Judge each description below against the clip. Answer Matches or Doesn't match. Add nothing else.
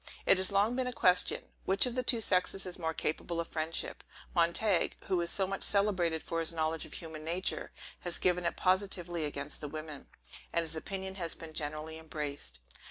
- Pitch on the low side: Doesn't match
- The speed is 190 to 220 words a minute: Matches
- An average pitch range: Matches